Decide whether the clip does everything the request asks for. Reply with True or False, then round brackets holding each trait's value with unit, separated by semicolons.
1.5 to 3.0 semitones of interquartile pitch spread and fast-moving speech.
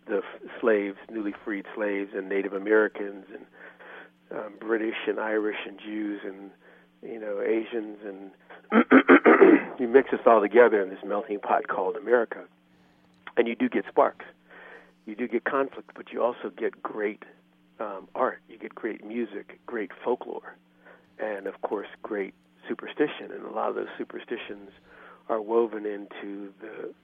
False (2.5 semitones; 155 wpm)